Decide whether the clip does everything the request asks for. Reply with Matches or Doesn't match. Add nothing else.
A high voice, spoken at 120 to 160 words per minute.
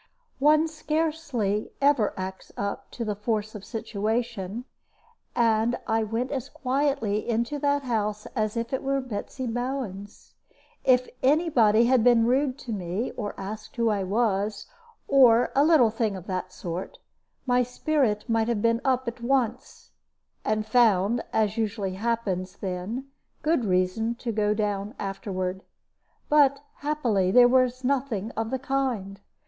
Matches